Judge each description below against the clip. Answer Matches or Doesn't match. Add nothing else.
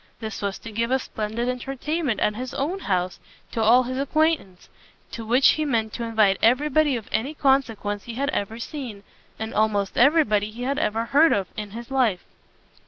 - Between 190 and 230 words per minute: Matches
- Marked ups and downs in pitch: Doesn't match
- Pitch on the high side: Matches